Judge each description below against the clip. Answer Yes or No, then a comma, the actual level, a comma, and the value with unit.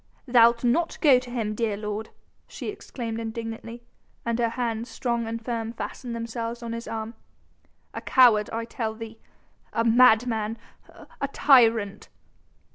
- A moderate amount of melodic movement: No, narrow, 1.2 semitones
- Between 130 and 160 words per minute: Yes, average, 140 wpm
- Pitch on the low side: No, high, 230 Hz